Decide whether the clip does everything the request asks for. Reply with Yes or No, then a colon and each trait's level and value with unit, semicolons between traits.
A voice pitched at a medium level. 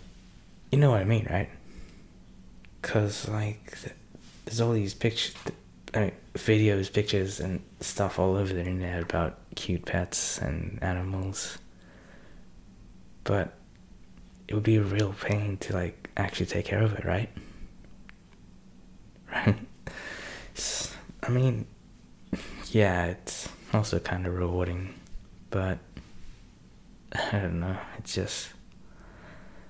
No: low, 100 Hz